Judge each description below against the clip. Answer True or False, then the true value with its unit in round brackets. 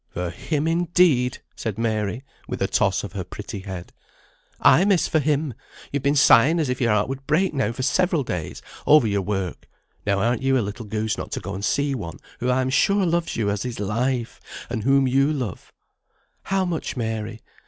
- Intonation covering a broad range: True (5.7 semitones)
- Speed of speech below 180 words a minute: False (205 wpm)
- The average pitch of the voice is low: True (125 Hz)